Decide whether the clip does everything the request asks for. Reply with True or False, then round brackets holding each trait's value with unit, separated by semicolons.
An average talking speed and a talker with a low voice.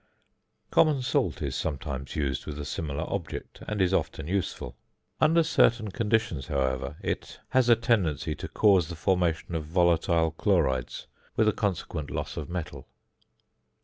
True (145 wpm; 85 Hz)